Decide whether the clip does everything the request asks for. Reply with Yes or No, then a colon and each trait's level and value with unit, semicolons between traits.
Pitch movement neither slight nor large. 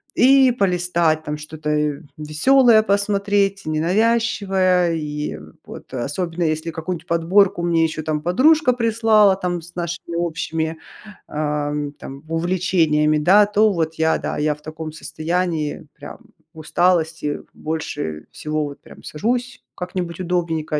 Yes: average, 4.0 semitones